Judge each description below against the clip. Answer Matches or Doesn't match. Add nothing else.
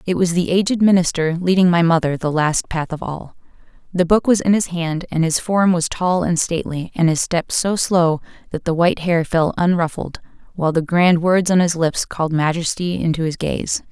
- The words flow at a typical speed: Doesn't match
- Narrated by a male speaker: Doesn't match